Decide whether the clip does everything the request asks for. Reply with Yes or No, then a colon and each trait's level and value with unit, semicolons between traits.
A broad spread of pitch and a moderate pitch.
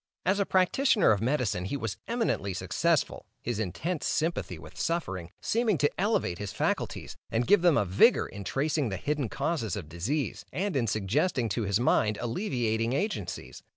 No: wide, 8.8 semitones; low, 130 Hz